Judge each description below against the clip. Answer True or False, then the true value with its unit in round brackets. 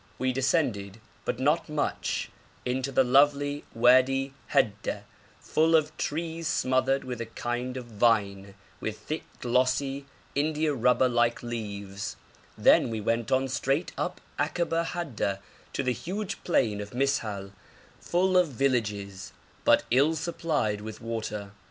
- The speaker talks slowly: True (130 wpm)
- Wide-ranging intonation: False (4.6 semitones)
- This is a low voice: True (130 Hz)